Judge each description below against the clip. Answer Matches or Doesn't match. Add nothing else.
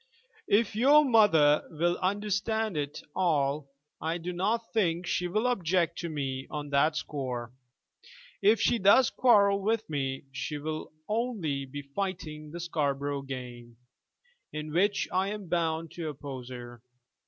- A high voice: Doesn't match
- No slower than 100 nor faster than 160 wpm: Matches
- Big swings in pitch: Matches